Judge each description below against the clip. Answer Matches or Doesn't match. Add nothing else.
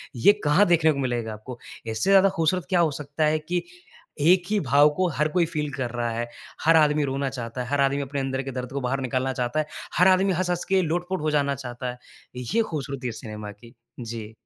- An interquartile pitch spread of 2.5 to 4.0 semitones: Doesn't match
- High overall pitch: Doesn't match